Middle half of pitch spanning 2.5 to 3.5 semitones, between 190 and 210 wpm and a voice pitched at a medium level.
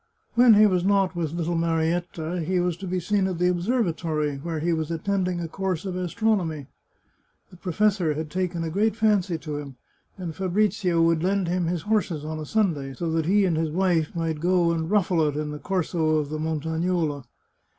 Yes: average, 2.8 semitones; average, 200 wpm; medium, 170 Hz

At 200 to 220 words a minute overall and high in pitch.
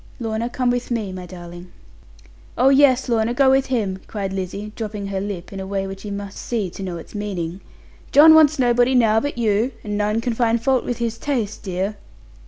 Yes: fast, 205 wpm; high, 215 Hz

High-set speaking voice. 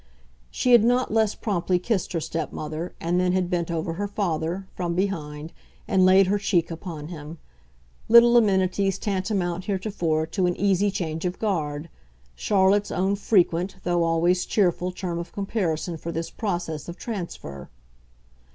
No: medium, 180 Hz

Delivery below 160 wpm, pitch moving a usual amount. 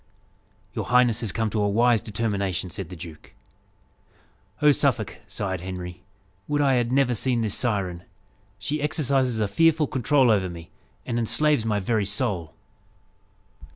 Yes: average, 150 wpm; average, 4.8 semitones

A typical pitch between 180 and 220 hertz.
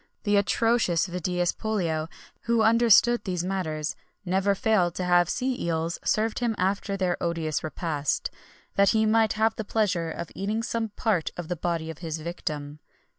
Yes: medium, 185 Hz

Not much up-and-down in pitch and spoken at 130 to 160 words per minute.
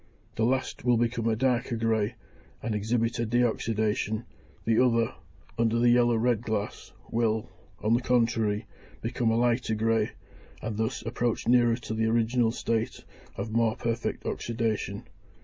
Yes: narrow, 1.4 semitones; average, 150 wpm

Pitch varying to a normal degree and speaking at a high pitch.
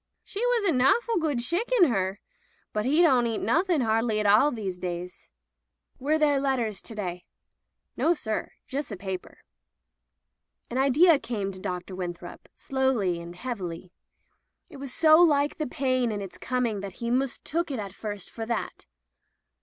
No: wide, 6.6 semitones; high, 240 Hz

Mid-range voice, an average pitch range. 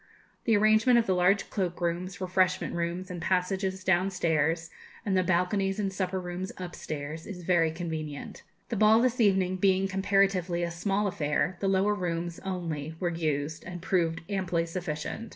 No: medium, 180 Hz; narrow, 2.3 semitones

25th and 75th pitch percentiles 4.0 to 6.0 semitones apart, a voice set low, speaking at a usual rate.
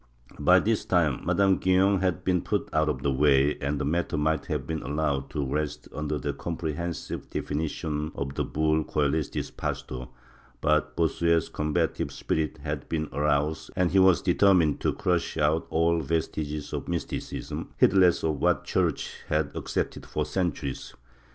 No: narrow, 2.6 semitones; very low, 80 Hz; average, 165 wpm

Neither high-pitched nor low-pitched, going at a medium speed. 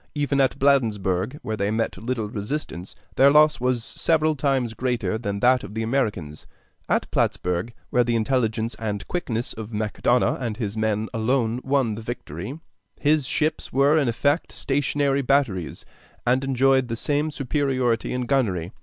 No: low, 120 Hz; average, 155 wpm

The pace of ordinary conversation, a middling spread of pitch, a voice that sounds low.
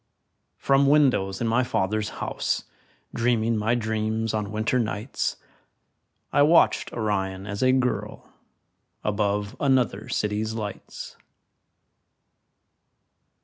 No: slow, 100 wpm; average, 3.0 semitones; low, 110 Hz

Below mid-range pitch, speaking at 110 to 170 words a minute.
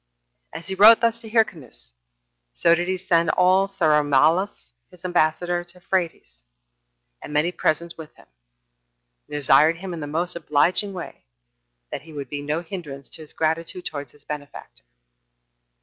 No: medium, 165 Hz; average, 160 wpm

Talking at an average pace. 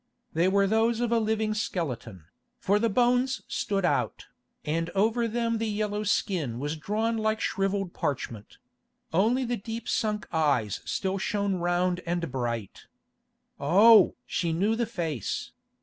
Yes: average, 145 wpm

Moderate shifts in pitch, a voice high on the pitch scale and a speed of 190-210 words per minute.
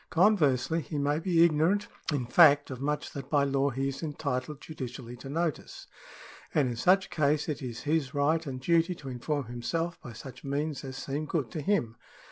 No: average, 3.4 semitones; medium, 145 Hz; average, 195 wpm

